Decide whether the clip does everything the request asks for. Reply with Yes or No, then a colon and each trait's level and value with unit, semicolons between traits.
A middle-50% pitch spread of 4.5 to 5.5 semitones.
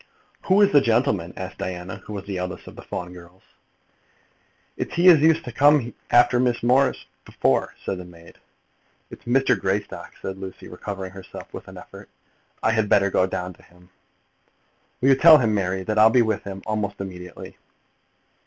Yes: average, 4.9 semitones